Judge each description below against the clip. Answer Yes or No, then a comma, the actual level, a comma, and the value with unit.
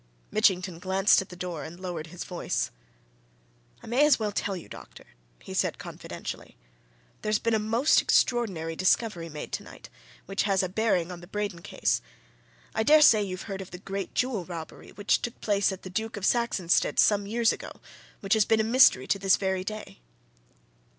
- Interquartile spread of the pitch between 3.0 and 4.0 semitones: Yes, average, 3.4 semitones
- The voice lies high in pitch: Yes, high, 195 Hz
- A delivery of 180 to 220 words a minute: Yes, average, 185 wpm